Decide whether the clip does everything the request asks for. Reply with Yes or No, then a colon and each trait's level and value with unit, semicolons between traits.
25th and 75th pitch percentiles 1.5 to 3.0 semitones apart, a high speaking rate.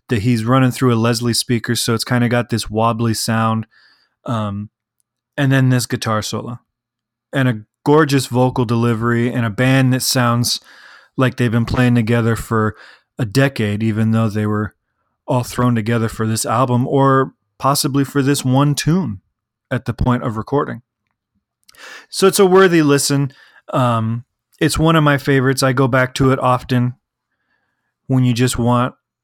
No: average, 2.7 semitones; average, 165 wpm